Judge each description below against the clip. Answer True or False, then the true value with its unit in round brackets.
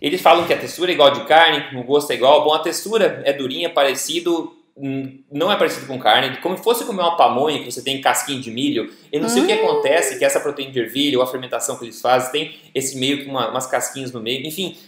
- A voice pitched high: False (145 Hz)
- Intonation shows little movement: False (5.2 semitones)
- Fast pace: True (260 wpm)